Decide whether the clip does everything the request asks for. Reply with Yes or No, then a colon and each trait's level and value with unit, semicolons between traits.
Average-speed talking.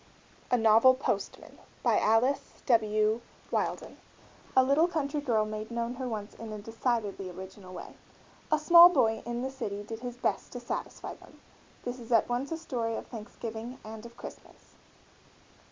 Yes: average, 165 wpm